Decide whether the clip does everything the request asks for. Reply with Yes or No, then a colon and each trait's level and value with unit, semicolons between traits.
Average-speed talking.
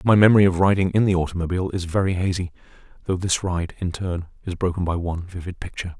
No: fast, 210 wpm